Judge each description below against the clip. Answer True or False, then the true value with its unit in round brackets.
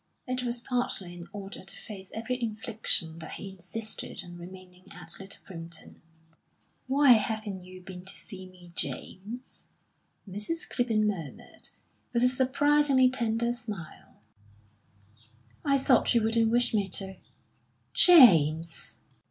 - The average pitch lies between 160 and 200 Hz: False (210 Hz)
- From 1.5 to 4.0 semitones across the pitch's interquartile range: False (4.9 semitones)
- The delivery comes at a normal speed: False (125 wpm)